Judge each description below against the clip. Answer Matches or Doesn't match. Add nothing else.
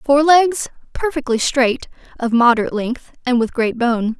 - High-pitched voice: Matches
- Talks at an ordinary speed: Matches